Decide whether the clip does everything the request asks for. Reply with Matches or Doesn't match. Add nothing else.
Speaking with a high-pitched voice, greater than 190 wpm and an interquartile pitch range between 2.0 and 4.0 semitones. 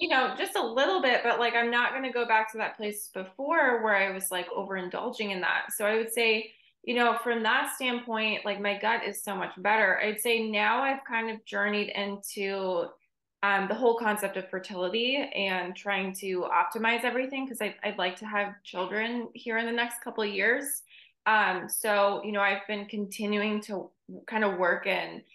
Matches